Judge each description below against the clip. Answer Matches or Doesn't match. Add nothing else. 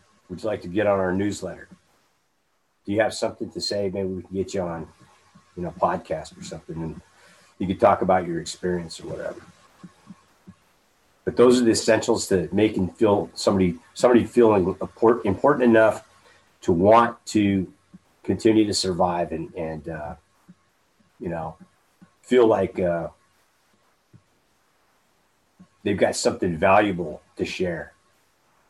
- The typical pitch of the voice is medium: Doesn't match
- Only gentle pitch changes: Doesn't match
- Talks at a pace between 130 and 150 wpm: Matches